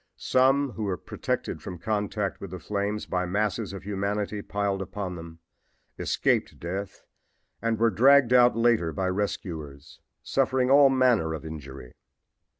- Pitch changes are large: No, average, 4.3 semitones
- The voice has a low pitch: Yes, low, 100 Hz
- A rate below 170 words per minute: Yes, average, 145 wpm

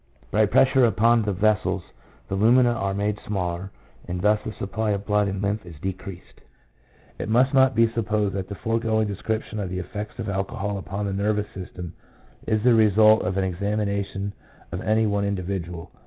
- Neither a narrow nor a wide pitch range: No, narrow, 2.0 semitones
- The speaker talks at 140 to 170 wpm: No, average, 185 wpm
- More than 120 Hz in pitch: No, low, 105 Hz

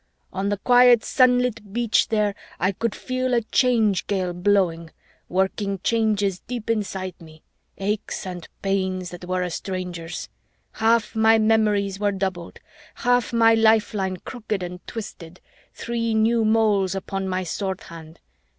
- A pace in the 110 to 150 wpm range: Yes, average, 140 wpm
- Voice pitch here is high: Yes, high, 200 Hz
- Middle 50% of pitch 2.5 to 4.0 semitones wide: Yes, average, 3.4 semitones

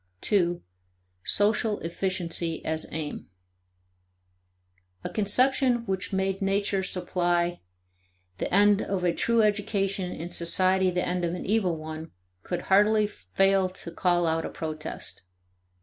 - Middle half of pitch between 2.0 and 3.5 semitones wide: Yes, average, 2.8 semitones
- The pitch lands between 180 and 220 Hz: Yes, medium, 185 Hz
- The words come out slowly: Yes, slow, 125 wpm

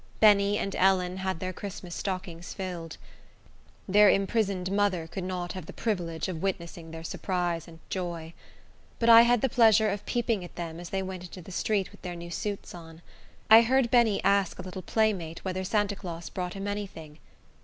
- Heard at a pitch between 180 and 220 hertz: Yes, medium, 185 Hz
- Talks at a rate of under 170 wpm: No, average, 190 wpm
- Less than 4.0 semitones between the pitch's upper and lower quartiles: Yes, average, 2.9 semitones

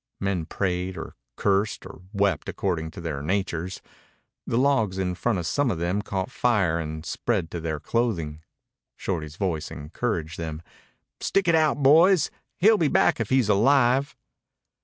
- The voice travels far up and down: Yes, wide, 6.6 semitones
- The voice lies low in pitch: Yes, very low, 95 Hz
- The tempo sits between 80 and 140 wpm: No, average, 160 wpm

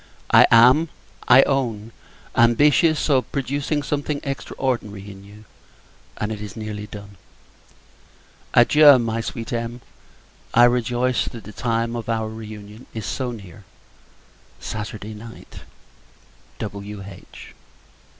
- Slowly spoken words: Yes, slow, 115 wpm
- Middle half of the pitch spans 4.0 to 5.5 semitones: No, average, 3.2 semitones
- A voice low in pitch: Yes, low, 115 Hz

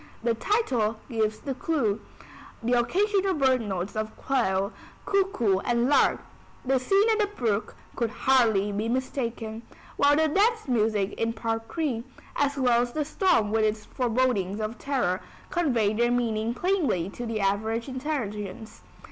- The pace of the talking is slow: No, average, 150 wpm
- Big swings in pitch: No, average, 4.5 semitones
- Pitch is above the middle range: Yes, high, 235 Hz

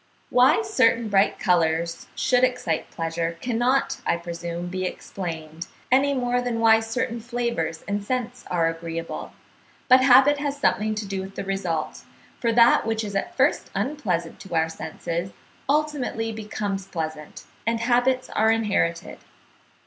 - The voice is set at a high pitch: Yes, high, 215 Hz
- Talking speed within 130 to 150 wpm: Yes, average, 145 wpm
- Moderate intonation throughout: No, wide, 6.4 semitones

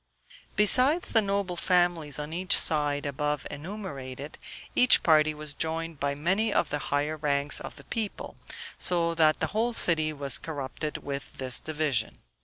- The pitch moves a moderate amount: Yes, average, 3.8 semitones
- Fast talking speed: No, average, 155 wpm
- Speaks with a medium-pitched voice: Yes, medium, 155 Hz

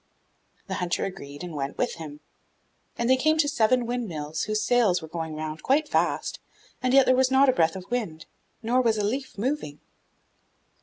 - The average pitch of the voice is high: Yes, high, 215 Hz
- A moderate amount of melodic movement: No, wide, 8.0 semitones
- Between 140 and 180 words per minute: No, average, 190 wpm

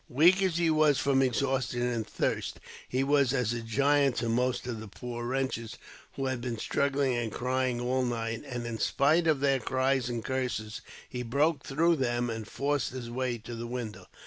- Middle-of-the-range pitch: No, low, 125 Hz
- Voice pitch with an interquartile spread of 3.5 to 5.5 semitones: No, narrow, 2.6 semitones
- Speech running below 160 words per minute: No, average, 195 wpm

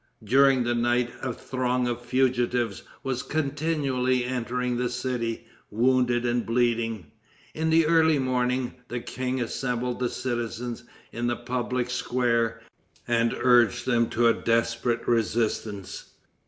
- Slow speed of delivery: Yes, slow, 125 wpm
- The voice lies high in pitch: No, low, 120 Hz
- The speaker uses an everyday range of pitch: No, narrow, 1.5 semitones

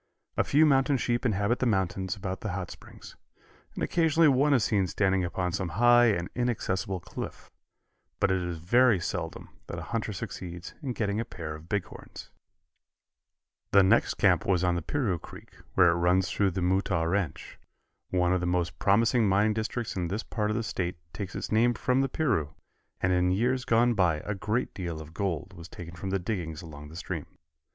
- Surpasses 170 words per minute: Yes, average, 195 wpm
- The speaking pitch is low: Yes, very low, 95 Hz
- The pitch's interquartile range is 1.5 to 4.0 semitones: No, average, 4.5 semitones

